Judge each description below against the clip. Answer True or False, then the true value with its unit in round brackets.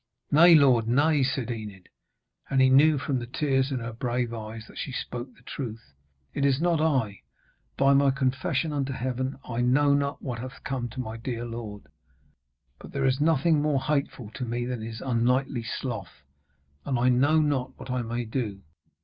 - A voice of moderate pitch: False (130 Hz)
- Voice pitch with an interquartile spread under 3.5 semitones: True (2.8 semitones)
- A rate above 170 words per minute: True (185 wpm)